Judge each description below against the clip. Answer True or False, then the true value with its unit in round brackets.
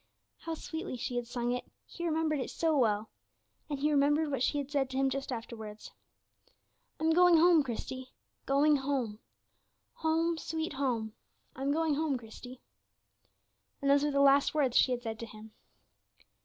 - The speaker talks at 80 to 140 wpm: False (170 wpm)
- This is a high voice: True (275 Hz)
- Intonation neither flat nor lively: True (4.0 semitones)